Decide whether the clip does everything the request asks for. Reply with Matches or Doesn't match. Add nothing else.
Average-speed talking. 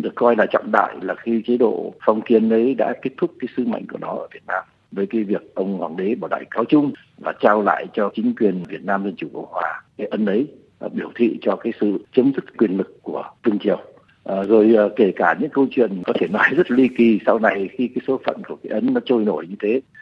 Doesn't match